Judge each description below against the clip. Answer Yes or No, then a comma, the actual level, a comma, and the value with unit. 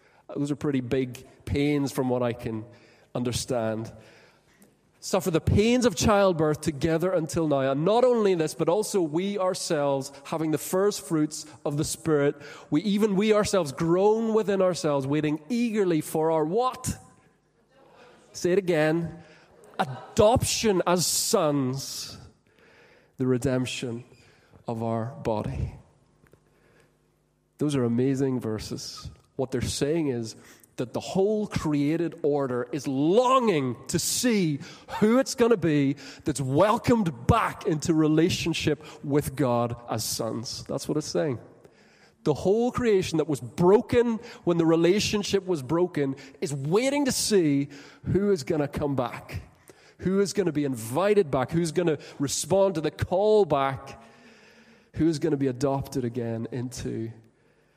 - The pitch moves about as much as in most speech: No, wide, 5.8 semitones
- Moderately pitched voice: Yes, medium, 155 Hz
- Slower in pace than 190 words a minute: Yes, average, 140 wpm